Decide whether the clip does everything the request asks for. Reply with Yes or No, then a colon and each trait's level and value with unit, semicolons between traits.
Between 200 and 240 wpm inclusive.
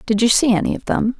No: fast, 300 wpm